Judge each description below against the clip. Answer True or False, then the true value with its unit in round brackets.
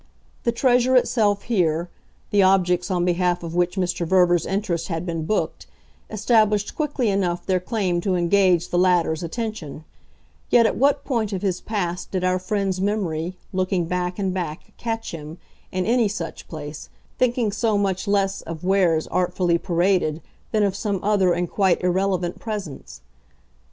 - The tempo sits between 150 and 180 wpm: True (160 wpm)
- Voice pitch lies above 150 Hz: True (185 Hz)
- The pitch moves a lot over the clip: False (2.9 semitones)